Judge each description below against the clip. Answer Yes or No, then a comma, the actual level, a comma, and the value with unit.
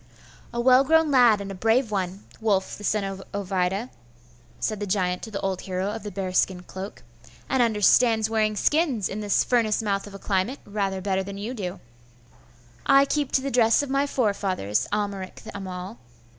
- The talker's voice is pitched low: No, high, 205 Hz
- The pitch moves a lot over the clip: No, average, 3.6 semitones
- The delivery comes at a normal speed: Yes, average, 185 wpm